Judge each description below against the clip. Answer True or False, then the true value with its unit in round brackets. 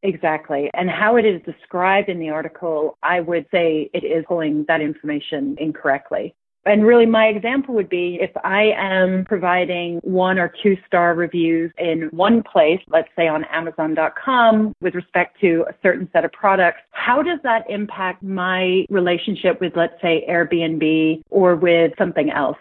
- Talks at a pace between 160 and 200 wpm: True (165 wpm)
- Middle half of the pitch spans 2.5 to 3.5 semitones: True (2.9 semitones)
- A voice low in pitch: False (175 Hz)